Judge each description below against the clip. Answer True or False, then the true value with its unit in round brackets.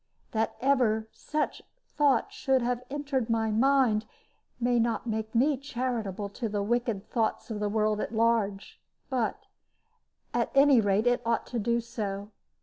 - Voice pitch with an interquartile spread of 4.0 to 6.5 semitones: False (3.0 semitones)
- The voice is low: False (230 Hz)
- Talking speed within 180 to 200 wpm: False (150 wpm)